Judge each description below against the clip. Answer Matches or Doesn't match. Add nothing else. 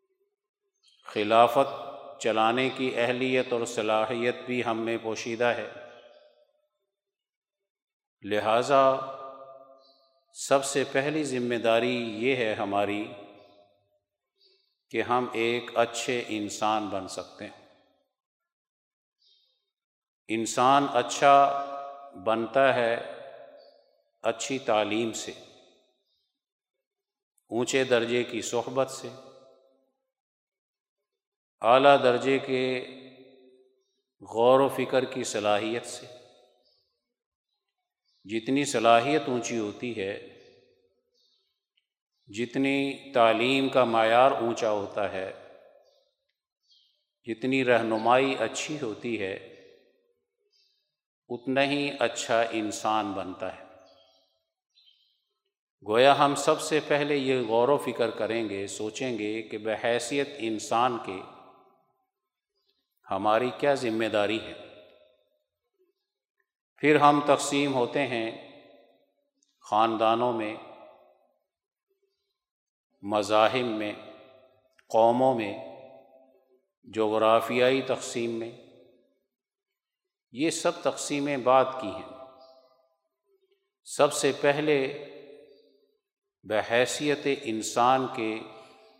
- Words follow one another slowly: Matches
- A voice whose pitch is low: Matches